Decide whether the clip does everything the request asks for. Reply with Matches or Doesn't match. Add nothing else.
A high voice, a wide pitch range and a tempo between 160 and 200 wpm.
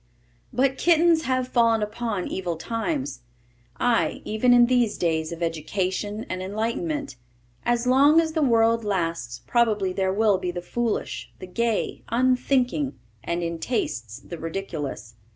Doesn't match